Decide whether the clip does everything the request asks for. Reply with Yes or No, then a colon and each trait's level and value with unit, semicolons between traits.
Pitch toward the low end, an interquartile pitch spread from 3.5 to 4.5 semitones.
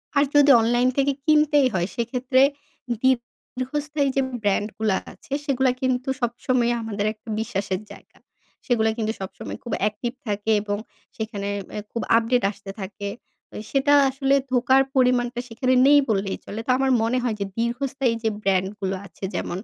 No: high, 240 Hz; average, 3.8 semitones